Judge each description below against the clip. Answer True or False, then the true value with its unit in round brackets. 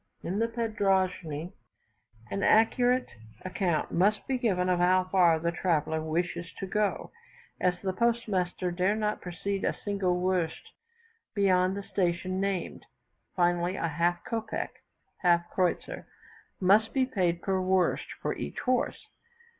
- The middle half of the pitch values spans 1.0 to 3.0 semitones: True (2.6 semitones)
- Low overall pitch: False (185 Hz)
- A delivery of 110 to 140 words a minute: True (135 wpm)